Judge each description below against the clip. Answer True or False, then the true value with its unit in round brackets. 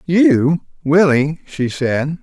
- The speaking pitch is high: False (150 Hz)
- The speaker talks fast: False (110 wpm)